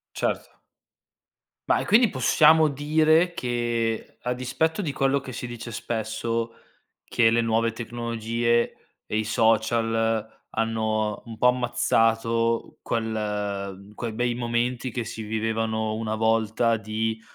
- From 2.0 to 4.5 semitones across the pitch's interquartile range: No, narrow, 1.6 semitones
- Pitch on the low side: Yes, low, 115 Hz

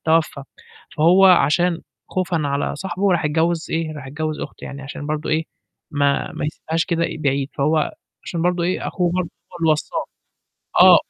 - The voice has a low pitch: No, medium, 160 Hz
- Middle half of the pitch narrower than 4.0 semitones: Yes, narrow, 2.6 semitones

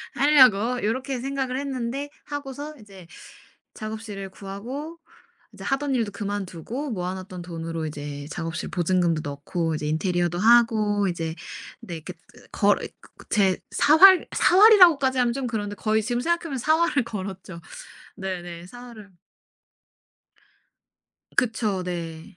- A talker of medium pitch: No, high, 215 Hz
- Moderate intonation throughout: No, wide, 6.8 semitones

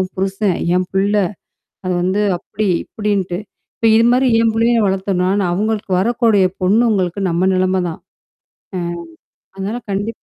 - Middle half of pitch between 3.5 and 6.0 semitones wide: No, average, 3.0 semitones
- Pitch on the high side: Yes, high, 195 Hz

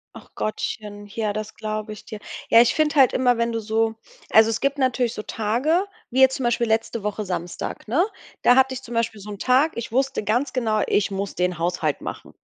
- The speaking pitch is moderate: No, high, 225 Hz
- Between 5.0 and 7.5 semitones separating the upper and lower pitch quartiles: No, average, 3.3 semitones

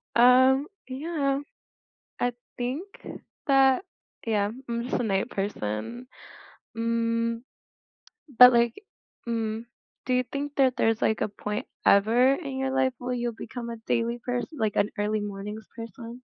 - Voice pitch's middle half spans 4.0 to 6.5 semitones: No, average, 2.9 semitones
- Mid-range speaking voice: No, high, 235 Hz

